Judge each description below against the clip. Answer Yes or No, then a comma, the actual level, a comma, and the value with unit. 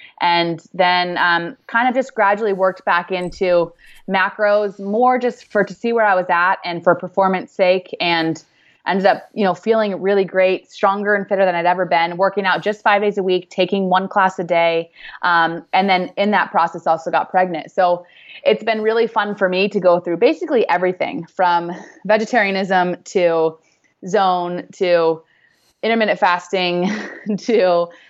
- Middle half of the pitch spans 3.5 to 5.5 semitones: No, average, 2.9 semitones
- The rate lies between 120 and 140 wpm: No, average, 170 wpm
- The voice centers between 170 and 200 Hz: Yes, medium, 185 Hz